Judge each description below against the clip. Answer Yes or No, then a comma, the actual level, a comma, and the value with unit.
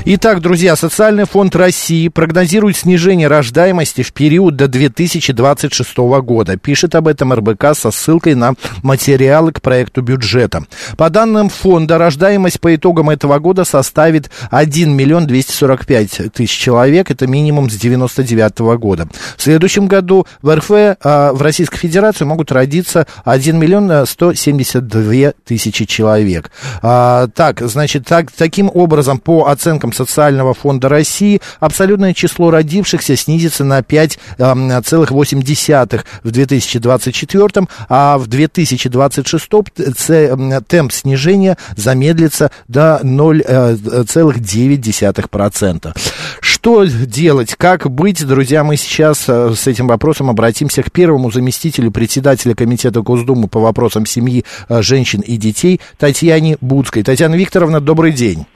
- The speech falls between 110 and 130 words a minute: Yes, average, 115 wpm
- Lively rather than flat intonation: No, average, 5.0 semitones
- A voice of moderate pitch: Yes, medium, 145 Hz